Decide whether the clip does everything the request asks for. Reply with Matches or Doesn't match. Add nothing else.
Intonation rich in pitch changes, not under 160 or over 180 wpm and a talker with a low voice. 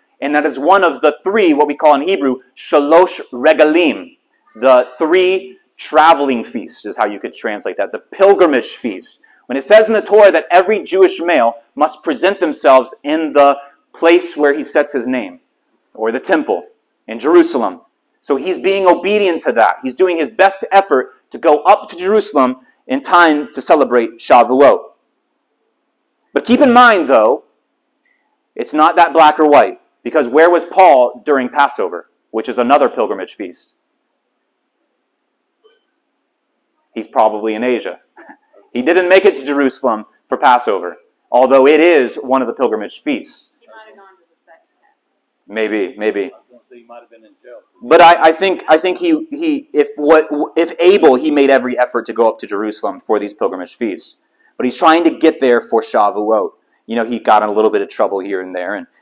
Doesn't match